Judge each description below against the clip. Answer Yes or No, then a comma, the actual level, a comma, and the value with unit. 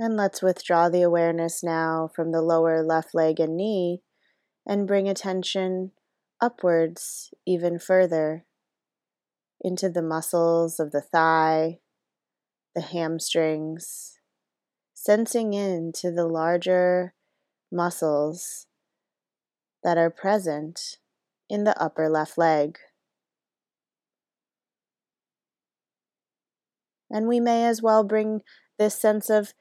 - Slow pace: Yes, slow, 100 wpm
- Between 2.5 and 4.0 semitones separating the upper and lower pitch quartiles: Yes, average, 3.6 semitones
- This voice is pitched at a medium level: Yes, medium, 175 Hz